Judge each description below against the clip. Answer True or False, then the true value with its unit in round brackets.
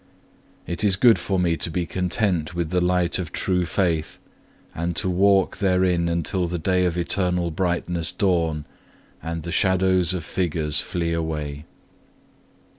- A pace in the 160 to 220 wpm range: False (150 wpm)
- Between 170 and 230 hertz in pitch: False (90 Hz)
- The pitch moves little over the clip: True (1.9 semitones)